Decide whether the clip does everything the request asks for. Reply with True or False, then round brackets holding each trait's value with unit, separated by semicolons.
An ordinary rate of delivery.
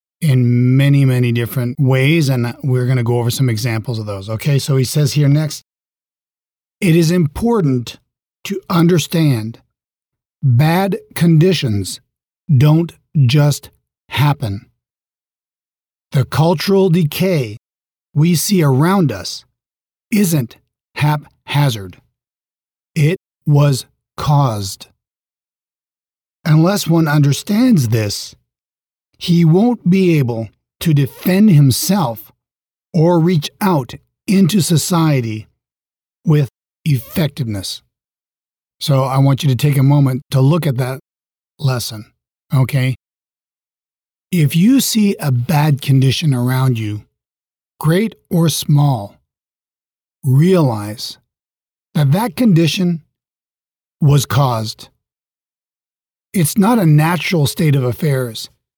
False (100 wpm)